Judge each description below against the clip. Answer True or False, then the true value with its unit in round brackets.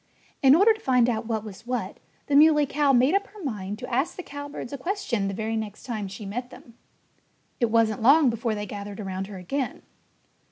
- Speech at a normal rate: False (210 wpm)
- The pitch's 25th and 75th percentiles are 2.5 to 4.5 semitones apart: False (5.2 semitones)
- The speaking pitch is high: True (240 Hz)